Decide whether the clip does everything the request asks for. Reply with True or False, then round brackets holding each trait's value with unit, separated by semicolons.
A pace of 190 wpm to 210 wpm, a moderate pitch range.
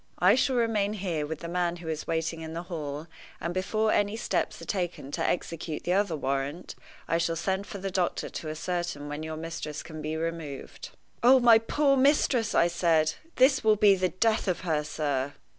True (200 wpm; 4.4 semitones)